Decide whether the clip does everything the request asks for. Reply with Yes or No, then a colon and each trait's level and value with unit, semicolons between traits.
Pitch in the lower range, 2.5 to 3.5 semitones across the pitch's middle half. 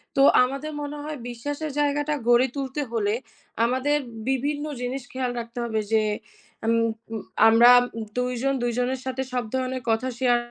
No: very high, 255 Hz; average, 2.8 semitones